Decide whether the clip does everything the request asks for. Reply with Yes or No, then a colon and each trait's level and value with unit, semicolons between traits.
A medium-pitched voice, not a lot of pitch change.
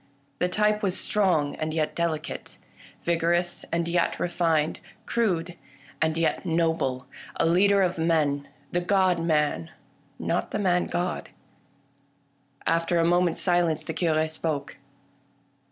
Yes: medium, 170 Hz; narrow, 2.0 semitones